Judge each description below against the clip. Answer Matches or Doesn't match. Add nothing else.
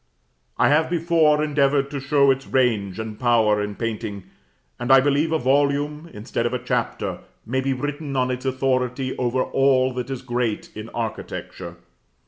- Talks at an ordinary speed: Matches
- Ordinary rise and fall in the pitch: Matches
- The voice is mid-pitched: Doesn't match